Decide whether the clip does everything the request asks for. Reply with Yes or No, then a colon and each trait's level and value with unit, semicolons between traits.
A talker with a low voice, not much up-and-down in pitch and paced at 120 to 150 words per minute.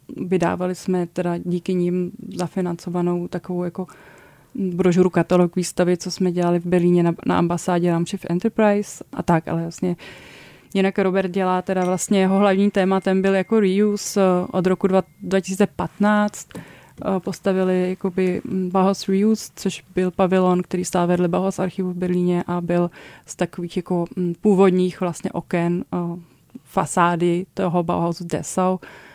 No: medium, 180 Hz; narrow, 1.5 semitones; average, 135 wpm